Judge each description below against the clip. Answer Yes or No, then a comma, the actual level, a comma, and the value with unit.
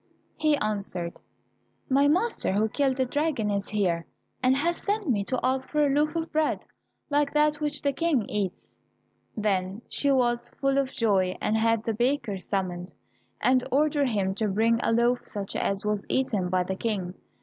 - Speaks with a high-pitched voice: Yes, high, 240 Hz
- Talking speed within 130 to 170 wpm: No, average, 180 wpm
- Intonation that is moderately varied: No, wide, 6.1 semitones